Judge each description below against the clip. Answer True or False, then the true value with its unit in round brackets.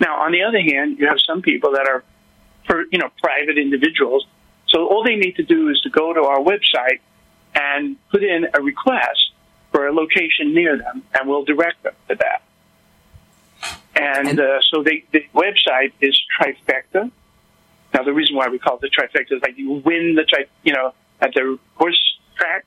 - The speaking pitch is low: False (155 Hz)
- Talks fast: False (195 wpm)